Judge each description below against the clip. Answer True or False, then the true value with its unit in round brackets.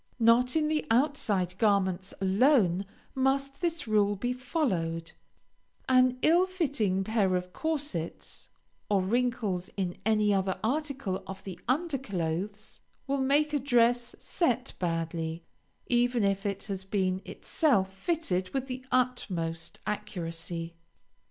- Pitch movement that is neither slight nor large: False (5.9 semitones)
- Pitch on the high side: True (215 Hz)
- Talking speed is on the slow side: True (125 wpm)